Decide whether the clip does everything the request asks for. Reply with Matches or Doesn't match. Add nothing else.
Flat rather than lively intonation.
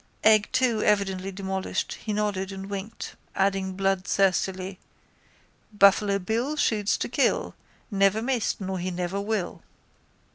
Matches